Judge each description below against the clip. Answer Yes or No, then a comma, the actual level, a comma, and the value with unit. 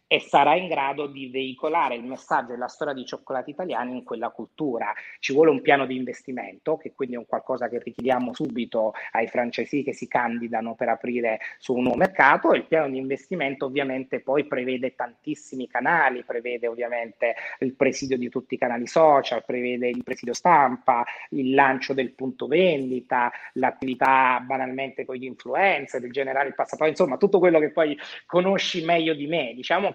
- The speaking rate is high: Yes, fast, 180 wpm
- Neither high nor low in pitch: No, low, 130 Hz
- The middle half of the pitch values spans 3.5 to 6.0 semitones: No, average, 2.8 semitones